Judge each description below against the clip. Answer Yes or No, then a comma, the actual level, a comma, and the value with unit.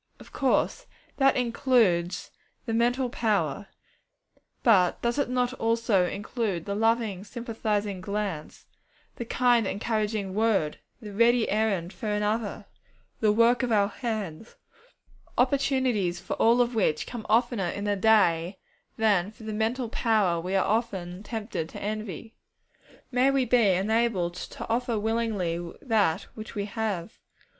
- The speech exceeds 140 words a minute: No, slow, 135 wpm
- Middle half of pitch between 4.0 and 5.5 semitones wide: No, average, 3.1 semitones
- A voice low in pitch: No, high, 215 Hz